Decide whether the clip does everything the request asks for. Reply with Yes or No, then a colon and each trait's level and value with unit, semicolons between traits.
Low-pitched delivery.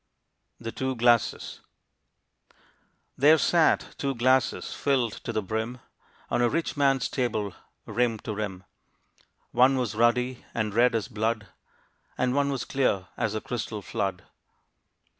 Yes: low, 120 Hz